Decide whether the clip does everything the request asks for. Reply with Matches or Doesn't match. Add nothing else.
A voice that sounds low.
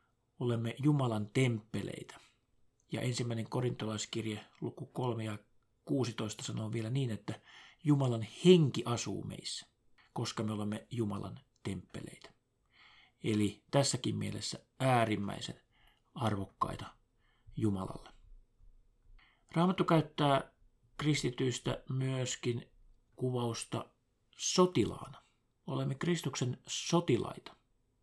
Matches